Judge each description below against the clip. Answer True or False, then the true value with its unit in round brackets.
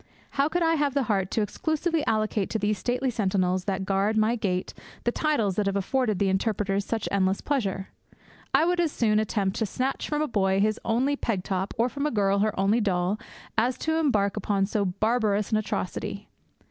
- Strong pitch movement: False (4.2 semitones)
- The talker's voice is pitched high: True (215 Hz)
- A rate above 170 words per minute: True (200 wpm)